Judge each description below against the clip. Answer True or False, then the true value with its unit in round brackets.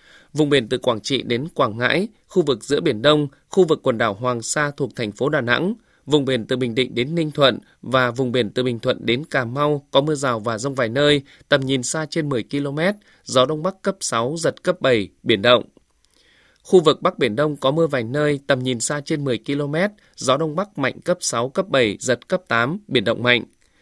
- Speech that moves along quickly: False (235 wpm)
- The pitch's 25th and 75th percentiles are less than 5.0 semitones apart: True (3.7 semitones)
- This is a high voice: False (140 Hz)